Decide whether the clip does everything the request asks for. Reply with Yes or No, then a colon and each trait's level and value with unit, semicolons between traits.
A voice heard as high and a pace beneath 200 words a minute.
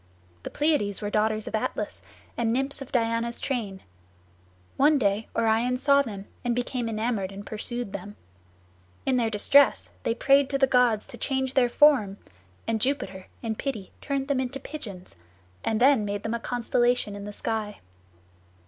Yes: high, 235 Hz; average, 165 wpm